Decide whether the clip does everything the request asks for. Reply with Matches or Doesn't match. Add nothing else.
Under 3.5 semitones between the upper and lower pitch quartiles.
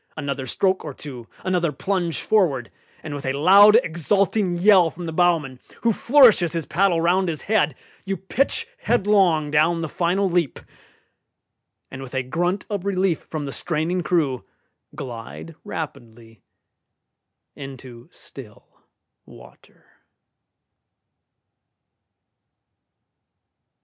Doesn't match